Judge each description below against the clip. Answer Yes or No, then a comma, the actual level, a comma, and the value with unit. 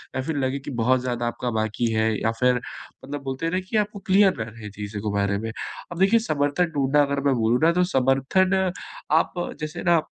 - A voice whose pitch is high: No, low, 135 Hz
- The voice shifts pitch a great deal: Yes, wide, 6.1 semitones